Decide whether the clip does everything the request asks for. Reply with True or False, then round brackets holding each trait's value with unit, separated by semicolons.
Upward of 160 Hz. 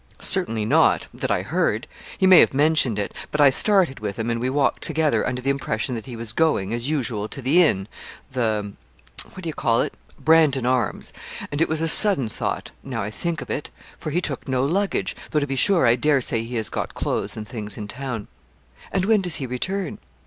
False (135 Hz)